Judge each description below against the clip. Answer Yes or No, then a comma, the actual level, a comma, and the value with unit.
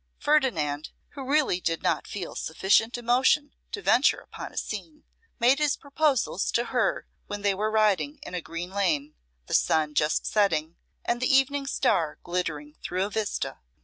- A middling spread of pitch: No, wide, 8.1 semitones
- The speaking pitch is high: Yes, high, 205 Hz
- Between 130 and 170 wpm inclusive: Yes, average, 165 wpm